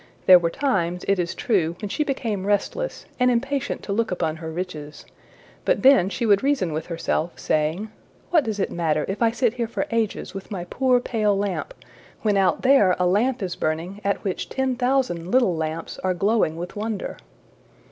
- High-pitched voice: Yes, high, 200 Hz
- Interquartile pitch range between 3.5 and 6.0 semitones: Yes, wide, 5.6 semitones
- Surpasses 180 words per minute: Yes, average, 190 wpm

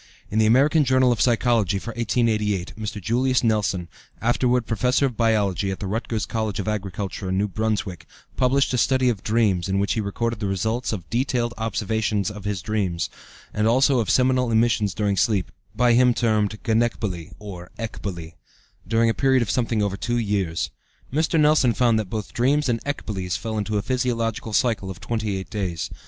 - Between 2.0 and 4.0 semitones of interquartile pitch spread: Yes, average, 3.2 semitones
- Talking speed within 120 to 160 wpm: No, average, 175 wpm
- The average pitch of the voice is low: Yes, low, 110 Hz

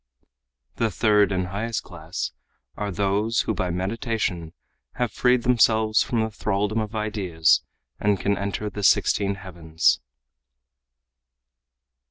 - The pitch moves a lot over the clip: No, average, 3.1 semitones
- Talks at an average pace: No, slow, 120 wpm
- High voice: No, low, 105 Hz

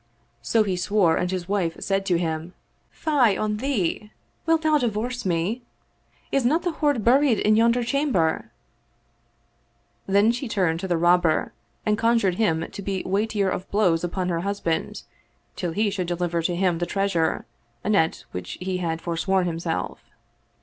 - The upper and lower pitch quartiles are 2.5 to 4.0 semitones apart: No, average, 4.5 semitones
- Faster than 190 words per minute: No, average, 165 wpm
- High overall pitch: Yes, high, 195 Hz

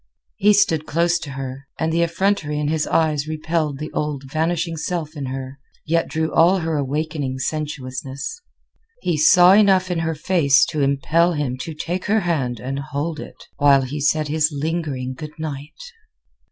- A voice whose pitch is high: No, medium, 155 Hz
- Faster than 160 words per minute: Yes, average, 170 wpm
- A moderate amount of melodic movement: Yes, average, 3.1 semitones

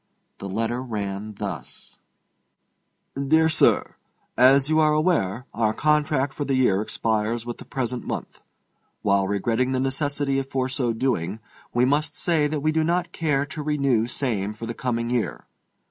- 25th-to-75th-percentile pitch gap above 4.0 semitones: Yes, average, 4.6 semitones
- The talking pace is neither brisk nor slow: Yes, average, 160 wpm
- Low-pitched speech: Yes, low, 130 Hz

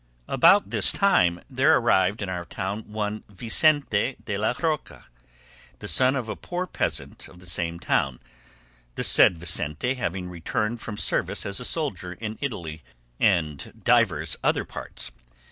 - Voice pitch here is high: No, low, 105 Hz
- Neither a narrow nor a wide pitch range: No, wide, 6.3 semitones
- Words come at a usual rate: Yes, average, 150 wpm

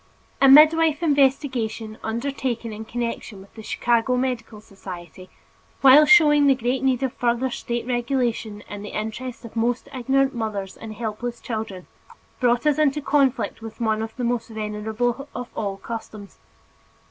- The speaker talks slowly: No, average, 155 wpm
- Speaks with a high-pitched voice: Yes, high, 240 Hz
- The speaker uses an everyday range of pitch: Yes, average, 3.3 semitones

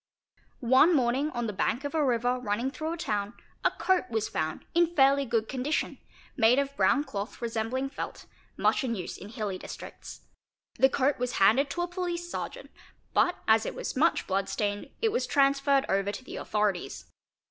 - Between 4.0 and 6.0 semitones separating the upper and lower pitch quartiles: Yes, average, 4.7 semitones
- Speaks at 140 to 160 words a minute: No, average, 185 wpm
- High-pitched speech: Yes, very high, 255 Hz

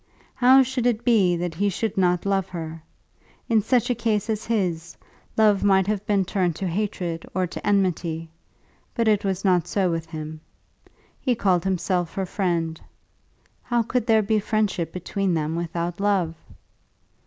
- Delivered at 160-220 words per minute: Yes, average, 165 wpm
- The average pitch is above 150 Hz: Yes, high, 190 Hz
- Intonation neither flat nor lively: Yes, average, 3.8 semitones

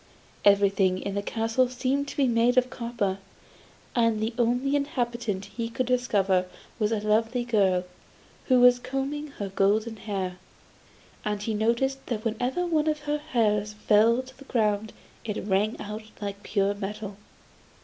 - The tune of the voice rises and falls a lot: No, average, 3.5 semitones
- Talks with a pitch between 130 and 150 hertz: No, high, 225 Hz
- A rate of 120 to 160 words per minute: Yes, average, 155 wpm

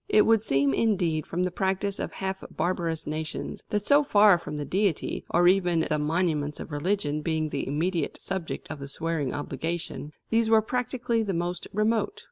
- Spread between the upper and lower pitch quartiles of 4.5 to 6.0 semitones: Yes, average, 4.8 semitones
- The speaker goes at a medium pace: Yes, average, 180 wpm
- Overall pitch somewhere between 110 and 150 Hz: No, medium, 175 Hz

